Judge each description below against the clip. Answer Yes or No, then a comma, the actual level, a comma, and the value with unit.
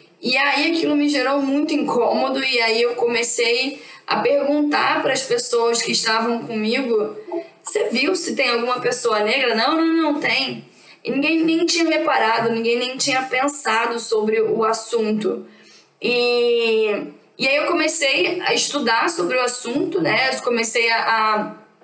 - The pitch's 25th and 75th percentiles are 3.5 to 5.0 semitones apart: Yes, average, 4.6 semitones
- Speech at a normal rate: Yes, average, 155 wpm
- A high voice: Yes, very high, 250 Hz